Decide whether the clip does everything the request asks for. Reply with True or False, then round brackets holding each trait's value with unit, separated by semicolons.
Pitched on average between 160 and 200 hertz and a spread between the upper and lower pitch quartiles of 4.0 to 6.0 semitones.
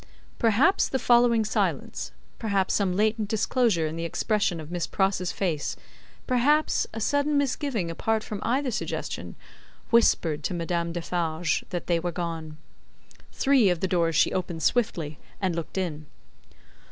True (190 Hz; 5.4 semitones)